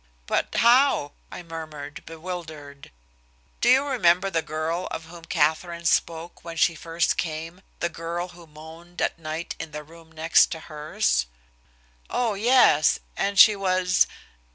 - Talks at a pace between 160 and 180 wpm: No, average, 140 wpm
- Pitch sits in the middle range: Yes, medium, 165 Hz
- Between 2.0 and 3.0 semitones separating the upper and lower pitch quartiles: Yes, narrow, 2.4 semitones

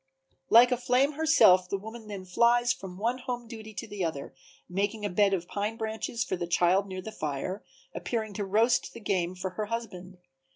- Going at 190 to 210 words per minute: Yes, average, 200 wpm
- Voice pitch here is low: No, high, 210 Hz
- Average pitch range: Yes, average, 3.9 semitones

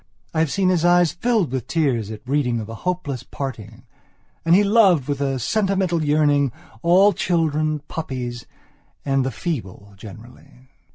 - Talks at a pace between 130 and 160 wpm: Yes, average, 155 wpm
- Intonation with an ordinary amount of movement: No, wide, 5.8 semitones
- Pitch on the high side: No, medium, 145 Hz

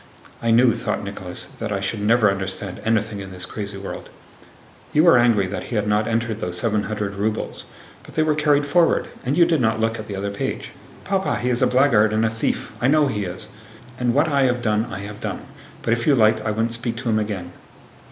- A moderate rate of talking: No, fast, 225 wpm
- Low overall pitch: Yes, low, 110 Hz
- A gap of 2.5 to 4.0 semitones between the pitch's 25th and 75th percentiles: Yes, average, 3.1 semitones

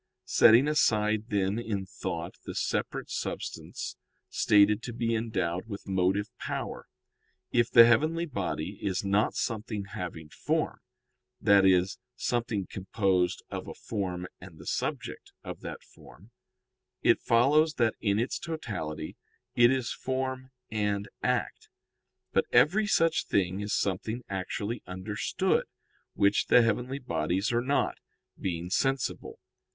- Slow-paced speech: Yes, slow, 130 wpm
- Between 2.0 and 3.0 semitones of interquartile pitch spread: No, average, 4.0 semitones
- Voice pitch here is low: Yes, low, 105 Hz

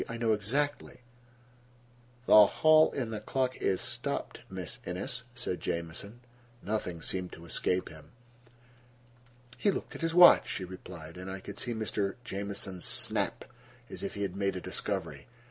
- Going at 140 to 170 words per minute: Yes, average, 155 wpm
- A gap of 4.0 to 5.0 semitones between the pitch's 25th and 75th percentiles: Yes, average, 4.7 semitones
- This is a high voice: No, low, 100 Hz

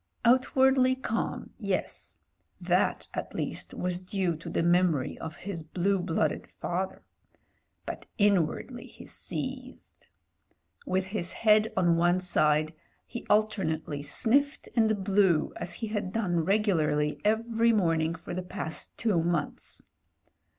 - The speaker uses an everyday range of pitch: Yes, average, 4.6 semitones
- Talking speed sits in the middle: No, slow, 130 wpm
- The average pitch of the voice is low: No, medium, 185 Hz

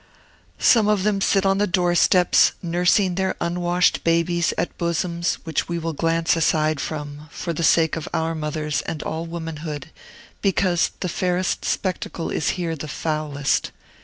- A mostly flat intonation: Yes, narrow, 2.2 semitones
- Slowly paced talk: No, average, 155 wpm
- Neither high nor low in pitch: Yes, medium, 170 Hz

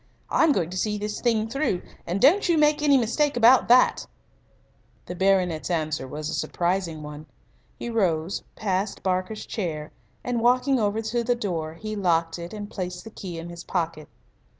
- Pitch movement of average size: No, wide, 5.7 semitones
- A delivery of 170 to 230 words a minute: Yes, average, 175 wpm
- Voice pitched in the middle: No, high, 195 Hz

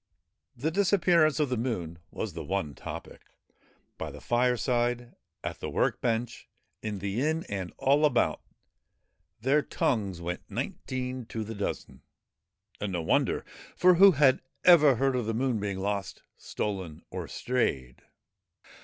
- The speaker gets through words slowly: No, average, 145 wpm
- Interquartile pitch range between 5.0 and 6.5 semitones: Yes, wide, 5.5 semitones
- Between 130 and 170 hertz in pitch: No, low, 120 Hz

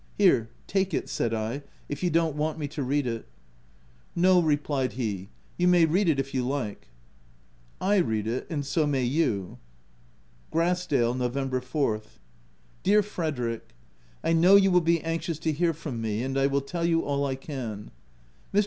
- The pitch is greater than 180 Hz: No, medium, 145 Hz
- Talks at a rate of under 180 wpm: No, average, 185 wpm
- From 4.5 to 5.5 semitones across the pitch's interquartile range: Yes, average, 5.2 semitones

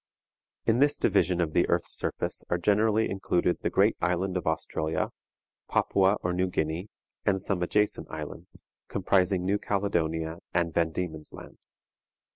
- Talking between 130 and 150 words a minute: Yes, average, 145 wpm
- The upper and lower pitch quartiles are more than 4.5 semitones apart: No, average, 3.1 semitones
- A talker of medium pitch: No, very low, 90 Hz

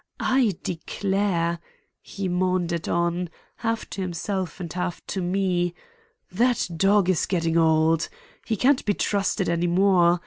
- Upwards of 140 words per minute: No, slow, 135 wpm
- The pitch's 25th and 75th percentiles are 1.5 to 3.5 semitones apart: Yes, narrow, 2.5 semitones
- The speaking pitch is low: No, medium, 180 Hz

